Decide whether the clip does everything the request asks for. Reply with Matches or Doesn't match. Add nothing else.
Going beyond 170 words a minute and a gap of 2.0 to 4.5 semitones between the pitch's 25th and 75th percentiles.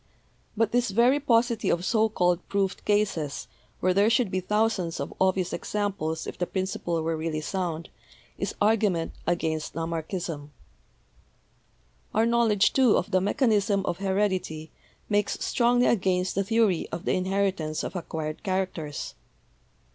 Doesn't match